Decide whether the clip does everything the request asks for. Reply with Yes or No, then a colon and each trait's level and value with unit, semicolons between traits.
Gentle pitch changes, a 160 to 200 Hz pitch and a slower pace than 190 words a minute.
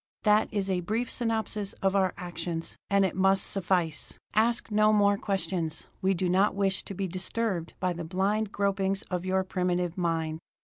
Yes: narrow, 2.2 semitones; high, 190 Hz; average, 170 wpm